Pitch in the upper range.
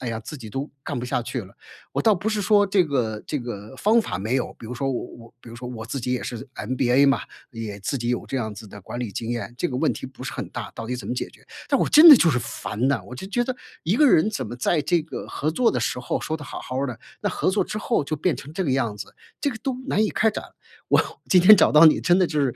No: low, 130 Hz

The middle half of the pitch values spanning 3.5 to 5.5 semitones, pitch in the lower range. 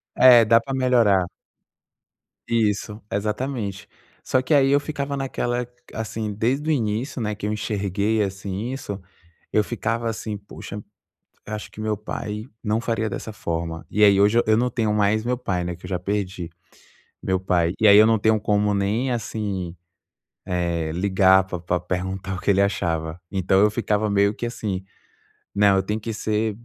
No: average, 2.9 semitones; low, 105 Hz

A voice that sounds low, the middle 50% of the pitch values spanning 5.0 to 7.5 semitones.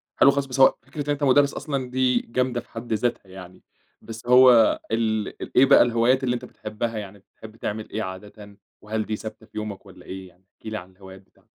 No: low, 110 Hz; average, 3.6 semitones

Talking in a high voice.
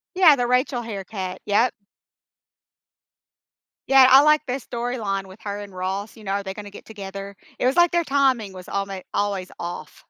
Yes: high, 205 Hz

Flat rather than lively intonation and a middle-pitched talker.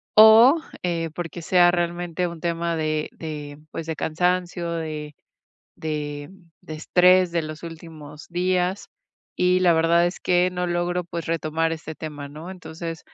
Yes: narrow, 2.1 semitones; medium, 170 Hz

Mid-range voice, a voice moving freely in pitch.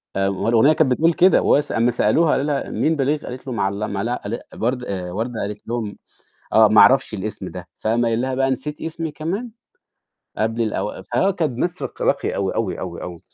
No: low, 120 Hz; wide, 5.7 semitones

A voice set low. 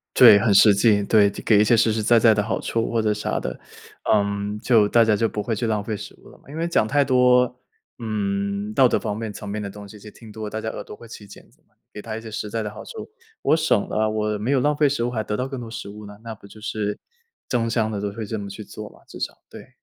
Yes: low, 110 Hz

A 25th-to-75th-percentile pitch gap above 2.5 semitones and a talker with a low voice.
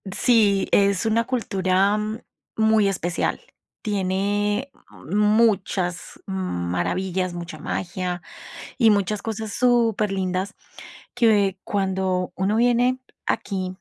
No: average, 2.9 semitones; high, 200 Hz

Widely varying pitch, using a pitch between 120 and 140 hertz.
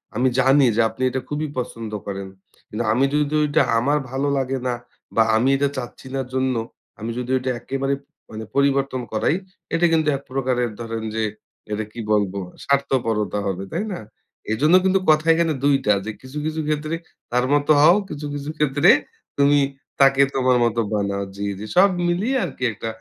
No: average, 4.2 semitones; low, 135 Hz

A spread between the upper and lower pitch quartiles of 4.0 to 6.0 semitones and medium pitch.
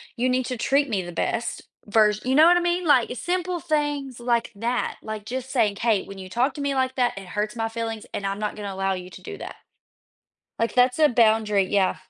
No: average, 4.3 semitones; high, 235 Hz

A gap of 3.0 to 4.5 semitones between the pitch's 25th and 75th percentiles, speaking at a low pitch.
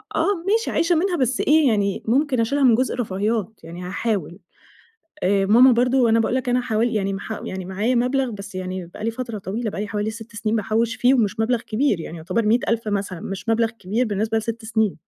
No: average, 3.5 semitones; high, 225 Hz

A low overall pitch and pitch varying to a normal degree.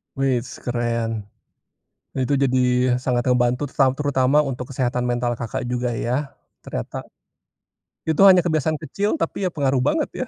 Yes: low, 130 Hz; average, 3.2 semitones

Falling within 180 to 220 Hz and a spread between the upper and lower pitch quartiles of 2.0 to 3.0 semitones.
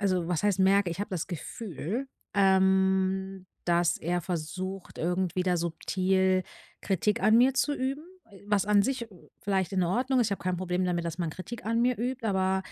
Yes: high, 190 Hz; narrow, 2.6 semitones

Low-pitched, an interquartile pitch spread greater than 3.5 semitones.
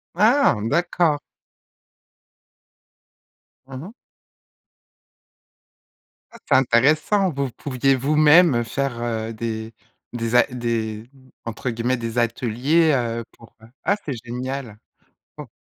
Yes: low, 125 Hz; average, 4.2 semitones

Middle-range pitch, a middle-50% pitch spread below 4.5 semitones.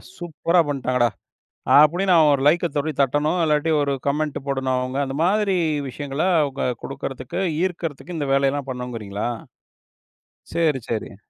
Yes: medium, 145 Hz; average, 3.5 semitones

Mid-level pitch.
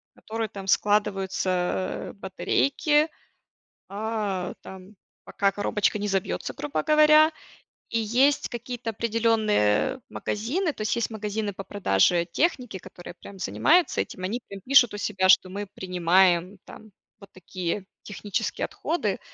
No: high, 205 Hz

